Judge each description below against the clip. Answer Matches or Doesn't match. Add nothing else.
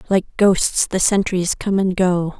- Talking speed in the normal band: Matches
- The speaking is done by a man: Doesn't match